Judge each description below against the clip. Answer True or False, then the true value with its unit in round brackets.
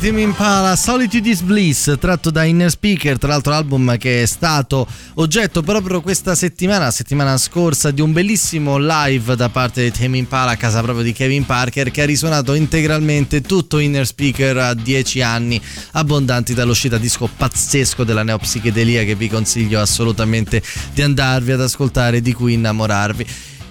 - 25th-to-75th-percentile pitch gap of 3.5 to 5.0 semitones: True (4.7 semitones)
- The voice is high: False (135 Hz)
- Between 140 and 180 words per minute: True (160 wpm)